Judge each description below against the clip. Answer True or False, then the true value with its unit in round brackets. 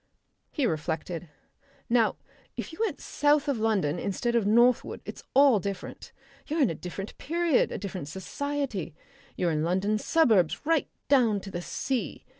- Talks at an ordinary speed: True (155 wpm)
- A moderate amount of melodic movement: False (7.5 semitones)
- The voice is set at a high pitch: True (215 Hz)